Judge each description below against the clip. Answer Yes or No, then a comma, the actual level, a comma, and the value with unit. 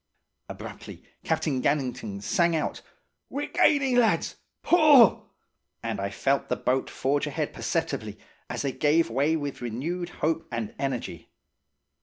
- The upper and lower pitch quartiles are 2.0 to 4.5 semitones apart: No, wide, 5.4 semitones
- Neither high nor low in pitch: Yes, medium, 145 Hz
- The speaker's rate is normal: No, slow, 130 wpm